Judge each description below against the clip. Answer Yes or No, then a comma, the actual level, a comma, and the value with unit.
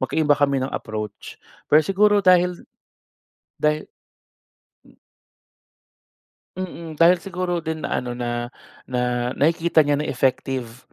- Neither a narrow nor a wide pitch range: No, wide, 5.7 semitones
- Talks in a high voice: No, medium, 150 Hz